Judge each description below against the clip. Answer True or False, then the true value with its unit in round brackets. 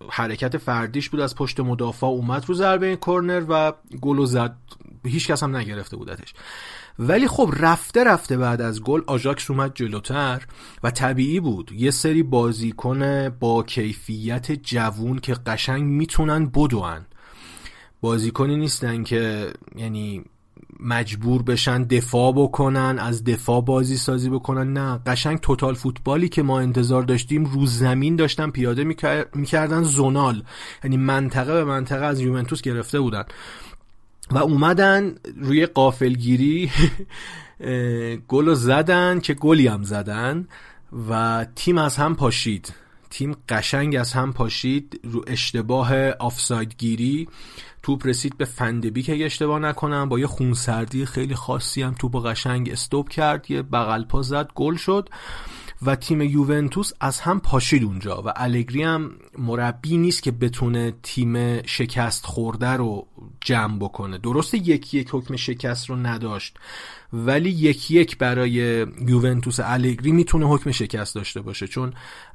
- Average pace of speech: True (135 wpm)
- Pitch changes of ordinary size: True (3.5 semitones)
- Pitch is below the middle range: True (130 Hz)